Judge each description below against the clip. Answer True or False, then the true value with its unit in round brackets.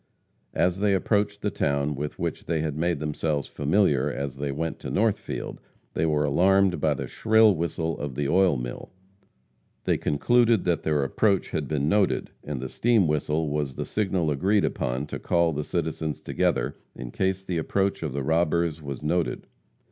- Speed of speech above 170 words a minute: True (180 wpm)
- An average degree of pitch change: True (4.6 semitones)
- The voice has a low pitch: True (80 Hz)